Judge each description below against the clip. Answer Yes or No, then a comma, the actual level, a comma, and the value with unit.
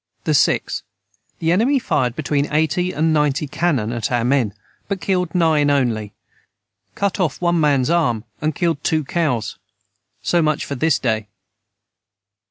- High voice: No, medium, 150 Hz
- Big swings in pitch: No, average, 4.8 semitones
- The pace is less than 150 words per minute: Yes, average, 140 wpm